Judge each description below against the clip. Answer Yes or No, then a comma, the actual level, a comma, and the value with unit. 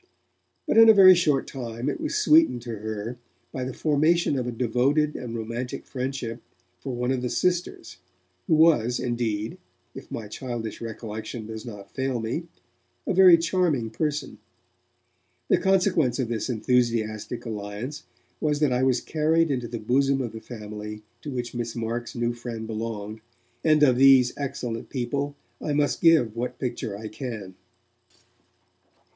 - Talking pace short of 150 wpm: No, average, 155 wpm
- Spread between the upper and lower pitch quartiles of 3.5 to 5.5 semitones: Yes, average, 4.3 semitones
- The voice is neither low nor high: No, low, 125 Hz